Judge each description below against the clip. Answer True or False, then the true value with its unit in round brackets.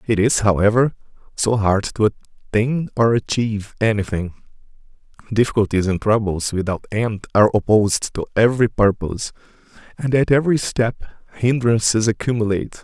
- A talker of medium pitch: False (110 Hz)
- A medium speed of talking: False (120 wpm)